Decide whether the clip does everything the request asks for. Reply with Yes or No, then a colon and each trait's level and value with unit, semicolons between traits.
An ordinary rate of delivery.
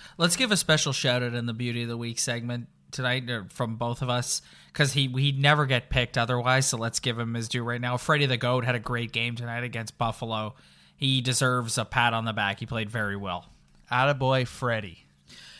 No: fast, 215 wpm